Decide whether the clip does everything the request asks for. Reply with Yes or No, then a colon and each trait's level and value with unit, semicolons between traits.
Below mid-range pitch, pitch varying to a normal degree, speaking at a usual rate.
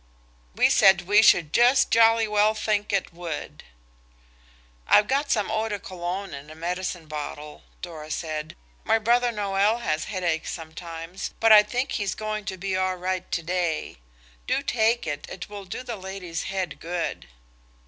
No: high, 190 Hz; average, 4.1 semitones; average, 165 wpm